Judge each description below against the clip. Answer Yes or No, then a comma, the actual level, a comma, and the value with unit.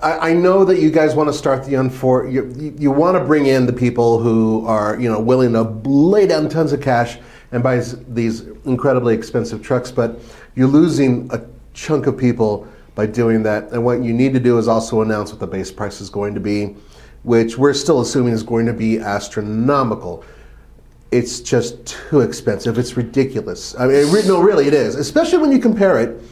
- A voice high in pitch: No, low, 120 Hz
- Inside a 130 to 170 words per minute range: No, fast, 205 wpm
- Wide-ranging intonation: No, average, 3.6 semitones